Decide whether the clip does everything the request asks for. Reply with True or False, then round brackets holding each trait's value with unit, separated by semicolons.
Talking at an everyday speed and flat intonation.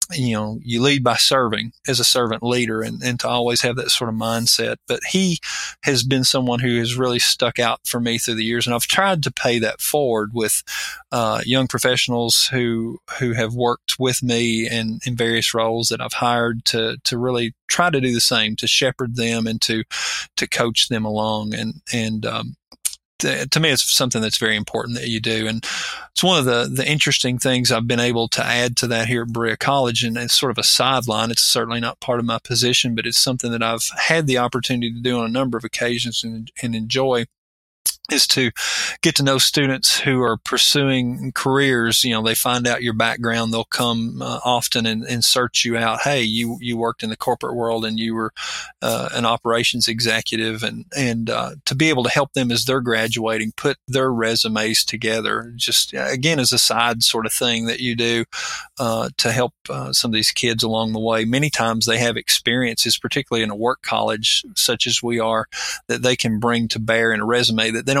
False (215 wpm; 1.8 semitones)